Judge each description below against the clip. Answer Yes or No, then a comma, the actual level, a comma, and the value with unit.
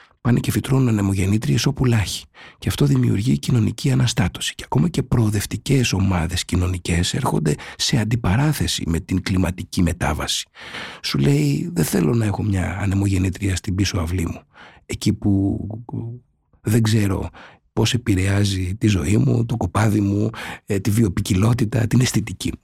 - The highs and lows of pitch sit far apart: No, average, 4.2 semitones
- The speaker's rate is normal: Yes, average, 135 wpm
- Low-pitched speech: Yes, low, 105 Hz